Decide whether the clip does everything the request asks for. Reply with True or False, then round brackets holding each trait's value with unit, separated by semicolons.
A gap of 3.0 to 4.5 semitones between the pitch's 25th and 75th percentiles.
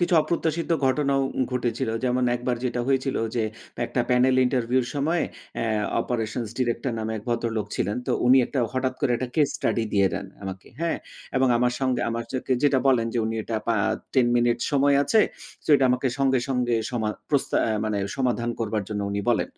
False (2.5 semitones)